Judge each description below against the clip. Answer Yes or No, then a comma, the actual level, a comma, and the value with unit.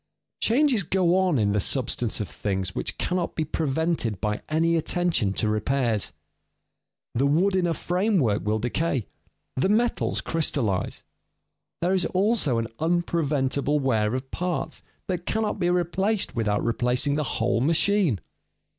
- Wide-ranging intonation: Yes, wide, 7.5 semitones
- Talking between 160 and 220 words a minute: No, average, 145 wpm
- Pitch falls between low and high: Yes, medium, 150 Hz